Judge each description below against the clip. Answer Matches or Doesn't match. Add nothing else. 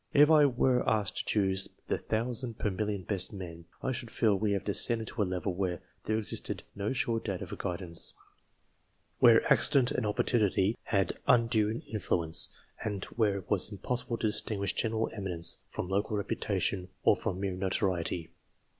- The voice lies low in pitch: Matches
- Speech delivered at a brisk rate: Doesn't match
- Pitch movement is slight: Doesn't match